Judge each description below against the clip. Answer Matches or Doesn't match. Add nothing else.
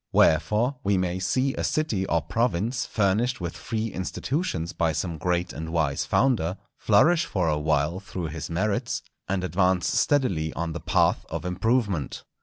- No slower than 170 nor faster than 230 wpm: Doesn't match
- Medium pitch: Doesn't match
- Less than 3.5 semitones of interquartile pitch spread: Doesn't match